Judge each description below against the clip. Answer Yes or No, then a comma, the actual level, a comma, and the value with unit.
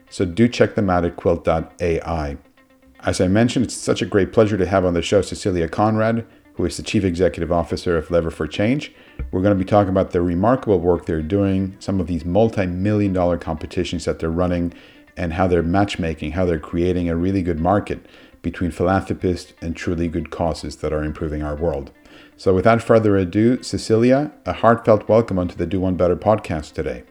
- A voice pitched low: Yes, very low, 90 Hz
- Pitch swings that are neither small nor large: Yes, average, 3.3 semitones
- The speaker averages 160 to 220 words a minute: Yes, average, 195 wpm